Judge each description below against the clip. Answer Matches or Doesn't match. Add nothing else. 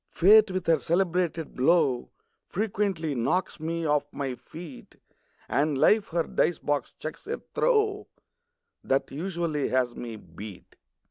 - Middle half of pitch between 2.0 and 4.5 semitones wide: Doesn't match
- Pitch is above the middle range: Doesn't match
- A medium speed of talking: Doesn't match